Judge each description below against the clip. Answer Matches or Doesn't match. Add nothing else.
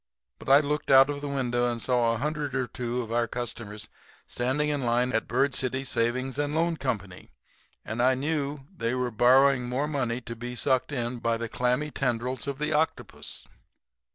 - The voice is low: Matches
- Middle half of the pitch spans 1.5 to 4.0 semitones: Matches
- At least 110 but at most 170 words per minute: Doesn't match